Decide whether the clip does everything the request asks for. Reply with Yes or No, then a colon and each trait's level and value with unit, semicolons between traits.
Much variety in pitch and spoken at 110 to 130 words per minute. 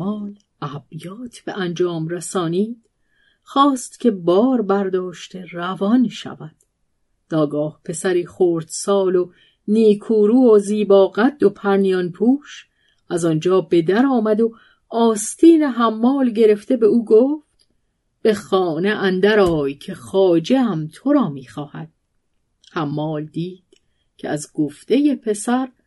No: average, 4.6 semitones; average, 120 wpm